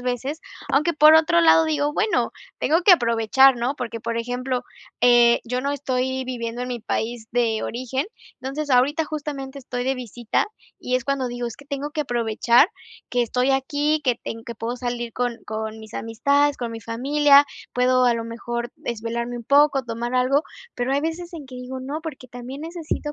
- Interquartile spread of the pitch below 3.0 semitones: No, average, 3.3 semitones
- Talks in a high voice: Yes, very high, 255 Hz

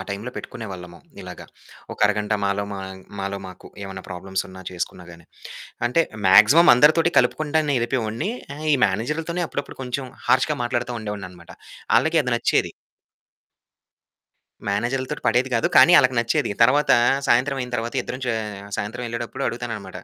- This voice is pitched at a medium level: No, low, 115 Hz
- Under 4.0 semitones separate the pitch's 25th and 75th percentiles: No, average, 5.3 semitones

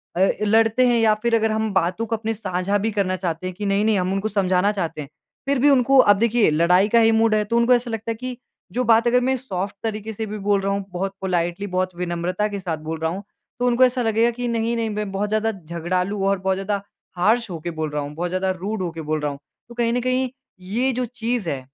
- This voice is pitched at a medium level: No, high, 205 Hz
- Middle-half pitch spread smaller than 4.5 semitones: Yes, average, 3.9 semitones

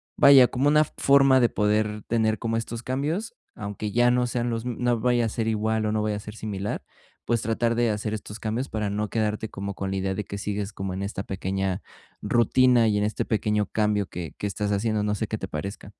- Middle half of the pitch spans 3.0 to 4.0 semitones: No, narrow, 2.4 semitones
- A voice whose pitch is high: No, low, 110 Hz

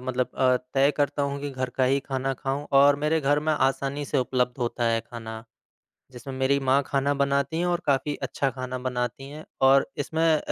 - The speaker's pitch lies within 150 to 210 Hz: No, low, 135 Hz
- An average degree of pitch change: No, narrow, 1.8 semitones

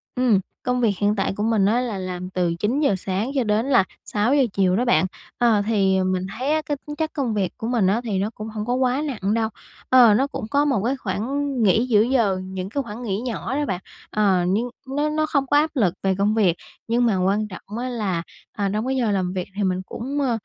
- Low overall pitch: No, high, 220 Hz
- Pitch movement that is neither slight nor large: Yes, average, 4.7 semitones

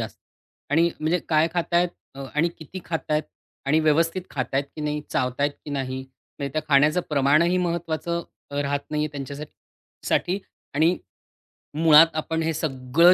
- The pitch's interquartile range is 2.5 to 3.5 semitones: Yes, average, 2.8 semitones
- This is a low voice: No, medium, 155 Hz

